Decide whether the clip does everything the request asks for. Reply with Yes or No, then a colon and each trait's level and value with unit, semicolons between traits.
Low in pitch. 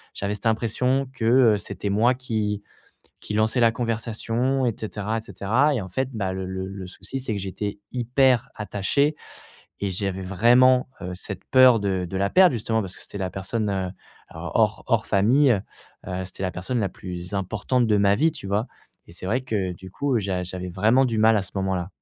Yes: low, 105 Hz